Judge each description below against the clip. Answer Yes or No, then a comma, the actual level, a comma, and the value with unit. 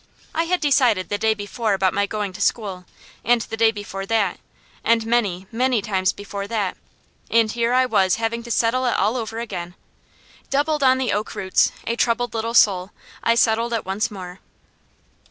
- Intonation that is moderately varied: Yes, average, 3.0 semitones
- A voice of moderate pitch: No, high, 225 Hz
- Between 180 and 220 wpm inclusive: Yes, average, 185 wpm